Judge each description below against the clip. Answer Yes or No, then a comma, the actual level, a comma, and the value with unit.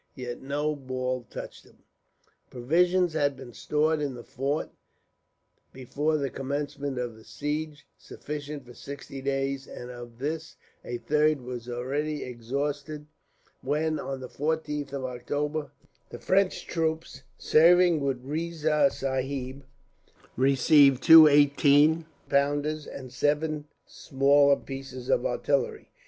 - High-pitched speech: No, medium, 140 Hz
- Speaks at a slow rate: Yes, slow, 120 wpm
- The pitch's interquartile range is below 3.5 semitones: Yes, narrow, 2.6 semitones